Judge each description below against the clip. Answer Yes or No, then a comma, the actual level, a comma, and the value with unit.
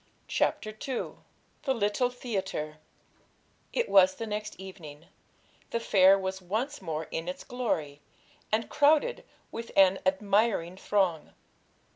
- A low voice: No, high, 195 Hz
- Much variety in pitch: No, average, 4.0 semitones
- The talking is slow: Yes, slow, 120 wpm